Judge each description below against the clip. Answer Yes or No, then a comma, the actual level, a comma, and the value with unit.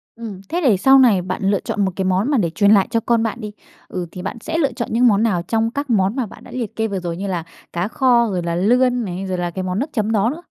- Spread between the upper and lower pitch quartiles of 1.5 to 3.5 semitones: No, average, 4.3 semitones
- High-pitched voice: Yes, high, 215 Hz